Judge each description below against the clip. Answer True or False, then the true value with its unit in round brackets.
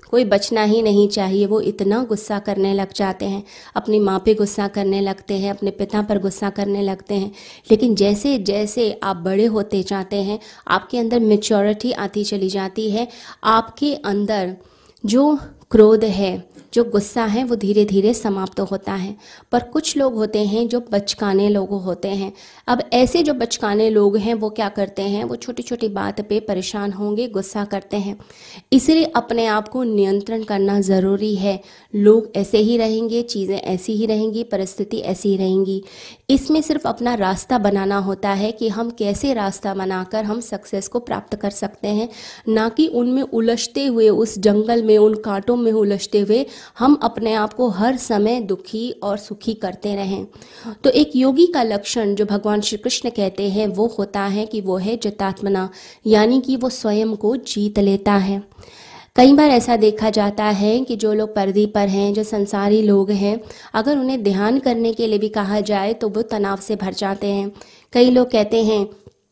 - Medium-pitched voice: False (210 Hz)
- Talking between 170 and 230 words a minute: True (185 wpm)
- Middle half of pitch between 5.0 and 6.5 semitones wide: False (2.4 semitones)